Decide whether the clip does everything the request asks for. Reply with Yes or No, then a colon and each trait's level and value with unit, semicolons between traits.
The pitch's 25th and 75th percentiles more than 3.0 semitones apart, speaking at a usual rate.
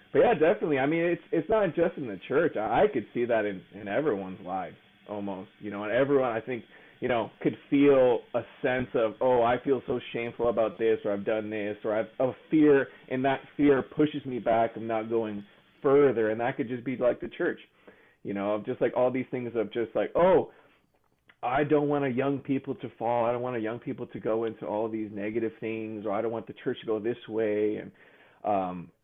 No: average, 3.7 semitones; fast, 235 wpm